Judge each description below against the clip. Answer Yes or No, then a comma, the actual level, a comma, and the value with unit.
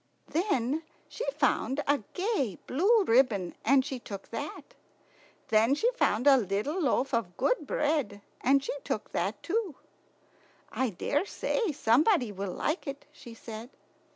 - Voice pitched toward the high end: Yes, very high, 270 Hz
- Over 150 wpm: No, average, 140 wpm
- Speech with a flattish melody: No, wide, 5.6 semitones